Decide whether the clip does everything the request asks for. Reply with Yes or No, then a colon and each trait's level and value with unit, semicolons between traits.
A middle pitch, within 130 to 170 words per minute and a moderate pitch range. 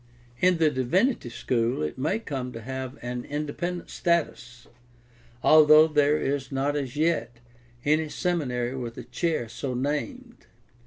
Yes: medium, 145 Hz; average, 140 wpm; average, 4.3 semitones